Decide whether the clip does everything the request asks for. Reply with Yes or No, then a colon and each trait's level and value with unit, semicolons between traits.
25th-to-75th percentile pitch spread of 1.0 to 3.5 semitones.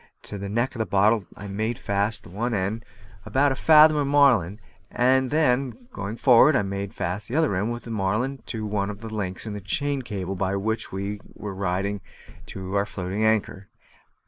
No: average, 3.9 semitones